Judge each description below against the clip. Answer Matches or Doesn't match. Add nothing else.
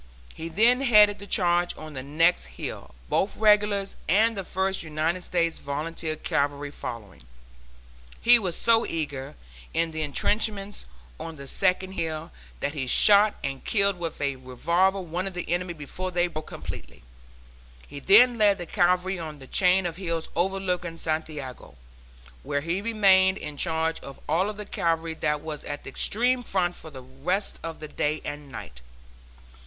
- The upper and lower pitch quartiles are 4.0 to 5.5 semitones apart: Matches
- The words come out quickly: Doesn't match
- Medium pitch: Matches